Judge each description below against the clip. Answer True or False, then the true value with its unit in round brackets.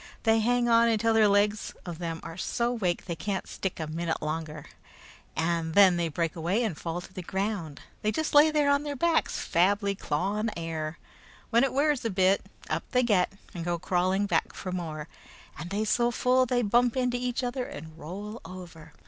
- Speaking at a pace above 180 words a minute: True (200 wpm)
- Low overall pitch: False (200 Hz)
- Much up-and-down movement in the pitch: True (5.9 semitones)